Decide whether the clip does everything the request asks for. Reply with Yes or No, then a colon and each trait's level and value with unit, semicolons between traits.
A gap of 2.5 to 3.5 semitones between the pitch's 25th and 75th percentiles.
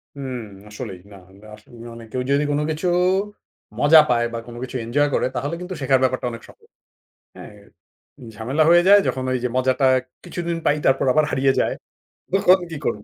No: average, 4.5 semitones